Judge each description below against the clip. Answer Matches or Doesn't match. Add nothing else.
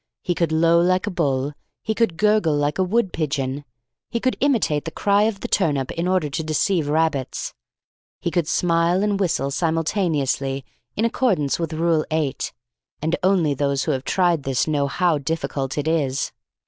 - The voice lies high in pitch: Doesn't match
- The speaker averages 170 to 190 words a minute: Matches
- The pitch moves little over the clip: Doesn't match